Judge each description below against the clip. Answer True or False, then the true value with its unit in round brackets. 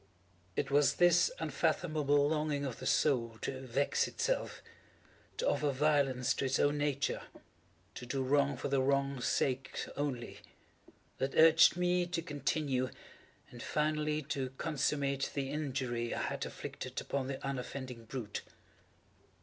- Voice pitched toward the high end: False (140 Hz)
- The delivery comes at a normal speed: False (125 wpm)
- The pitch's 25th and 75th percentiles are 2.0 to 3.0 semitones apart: True (2.5 semitones)